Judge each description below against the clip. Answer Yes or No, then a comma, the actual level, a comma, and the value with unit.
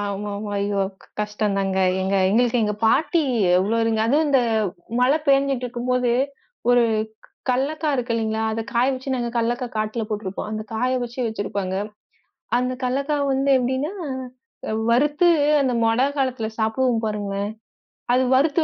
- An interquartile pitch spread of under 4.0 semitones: Yes, average, 3.5 semitones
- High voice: Yes, high, 240 Hz